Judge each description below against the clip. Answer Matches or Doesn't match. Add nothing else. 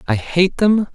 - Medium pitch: Matches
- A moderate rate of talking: Matches